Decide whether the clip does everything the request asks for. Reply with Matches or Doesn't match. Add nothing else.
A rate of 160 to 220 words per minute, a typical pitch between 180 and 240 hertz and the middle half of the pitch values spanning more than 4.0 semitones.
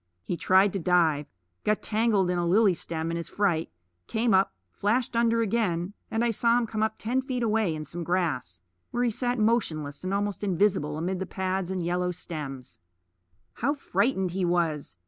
Matches